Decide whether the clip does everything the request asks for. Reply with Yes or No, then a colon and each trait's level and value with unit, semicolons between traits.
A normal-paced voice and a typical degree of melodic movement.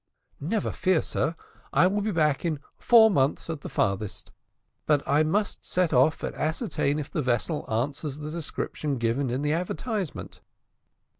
Yes: average, 165 wpm; average, 4.0 semitones